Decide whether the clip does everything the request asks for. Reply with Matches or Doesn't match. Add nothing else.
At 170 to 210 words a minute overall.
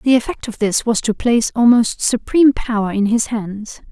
Matches